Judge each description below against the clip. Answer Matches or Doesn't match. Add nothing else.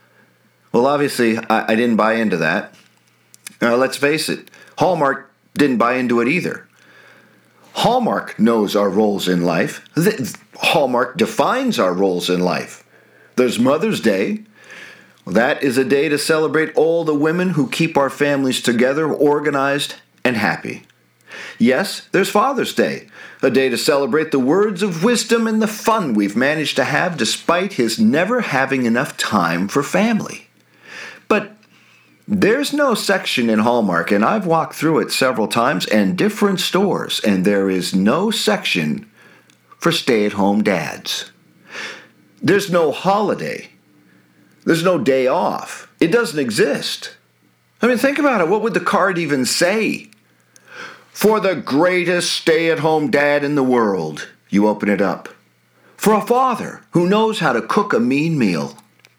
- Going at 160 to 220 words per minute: Doesn't match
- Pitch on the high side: Doesn't match